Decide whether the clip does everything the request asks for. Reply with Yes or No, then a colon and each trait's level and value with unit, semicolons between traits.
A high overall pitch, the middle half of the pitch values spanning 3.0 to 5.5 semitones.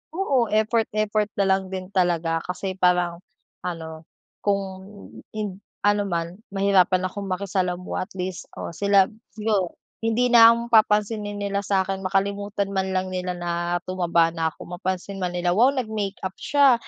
No: high, 195 Hz; narrow, 2.5 semitones